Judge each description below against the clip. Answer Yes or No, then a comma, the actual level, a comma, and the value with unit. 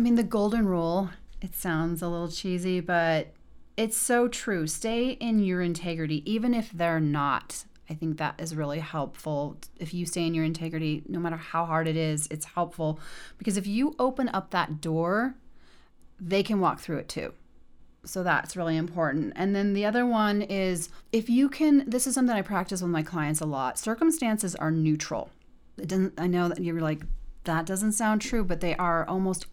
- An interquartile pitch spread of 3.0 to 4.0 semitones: No, average, 4.7 semitones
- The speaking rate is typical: Yes, average, 195 wpm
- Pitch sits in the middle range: Yes, medium, 175 Hz